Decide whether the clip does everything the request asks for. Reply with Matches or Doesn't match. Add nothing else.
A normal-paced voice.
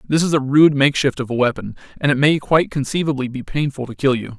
Doesn't match